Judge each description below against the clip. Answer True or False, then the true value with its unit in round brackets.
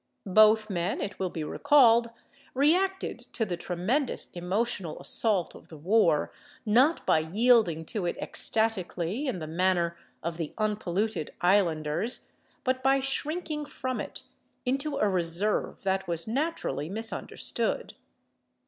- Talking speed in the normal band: False (130 wpm)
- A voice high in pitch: True (210 Hz)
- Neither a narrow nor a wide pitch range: False (6.6 semitones)